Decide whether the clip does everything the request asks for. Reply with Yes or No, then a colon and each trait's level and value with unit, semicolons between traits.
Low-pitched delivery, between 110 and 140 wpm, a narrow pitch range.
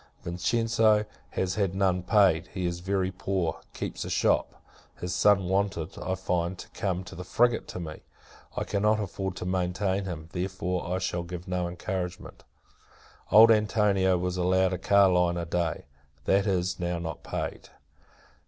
No: very low, 95 Hz; average, 160 wpm; narrow, 1.9 semitones